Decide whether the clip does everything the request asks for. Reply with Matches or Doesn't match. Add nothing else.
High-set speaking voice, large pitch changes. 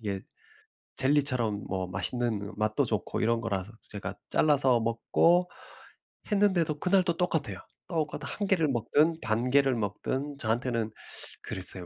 Doesn't match